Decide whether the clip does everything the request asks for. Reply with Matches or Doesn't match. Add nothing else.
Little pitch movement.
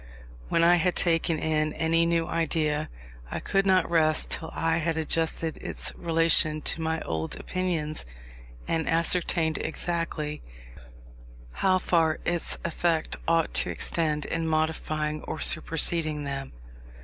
Matches